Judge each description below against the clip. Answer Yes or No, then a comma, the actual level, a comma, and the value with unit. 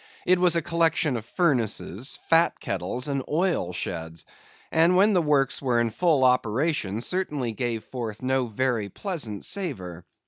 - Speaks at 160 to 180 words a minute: No, average, 150 wpm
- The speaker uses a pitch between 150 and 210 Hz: No, low, 130 Hz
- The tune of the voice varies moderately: No, wide, 6.8 semitones